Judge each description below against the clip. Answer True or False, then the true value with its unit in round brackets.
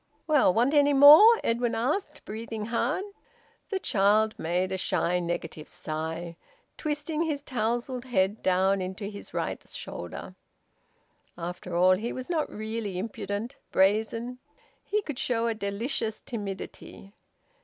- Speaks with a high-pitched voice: True (220 Hz)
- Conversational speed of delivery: False (130 wpm)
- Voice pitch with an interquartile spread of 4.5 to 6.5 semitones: True (5.3 semitones)